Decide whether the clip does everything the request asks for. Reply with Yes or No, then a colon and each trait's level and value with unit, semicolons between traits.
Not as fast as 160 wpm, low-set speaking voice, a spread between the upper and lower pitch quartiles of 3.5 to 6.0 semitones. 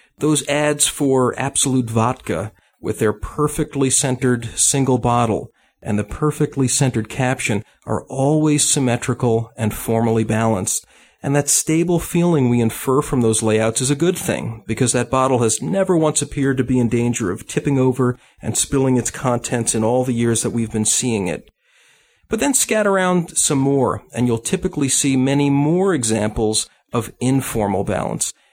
No: average, 165 wpm; low, 130 Hz; average, 4.1 semitones